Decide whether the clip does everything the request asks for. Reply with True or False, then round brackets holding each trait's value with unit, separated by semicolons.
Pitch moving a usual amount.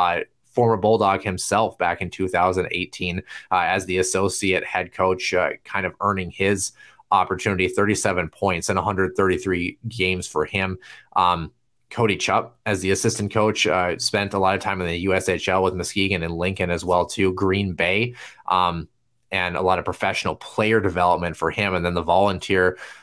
False (2.0 semitones)